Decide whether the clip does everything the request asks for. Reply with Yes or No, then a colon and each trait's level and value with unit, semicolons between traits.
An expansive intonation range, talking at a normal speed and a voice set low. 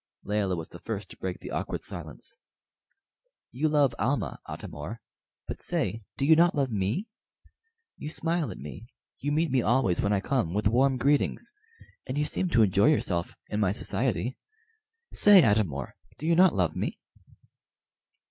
Yes: wide, 7.0 semitones; average, 170 wpm; low, 120 Hz